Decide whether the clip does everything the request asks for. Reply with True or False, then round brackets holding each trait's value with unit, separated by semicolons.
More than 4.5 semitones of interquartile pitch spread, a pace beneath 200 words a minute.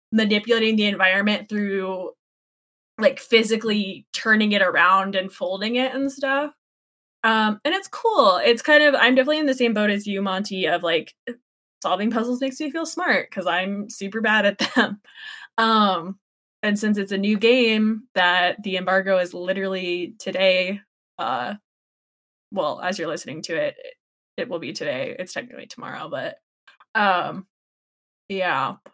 True (4.9 semitones; 155 wpm)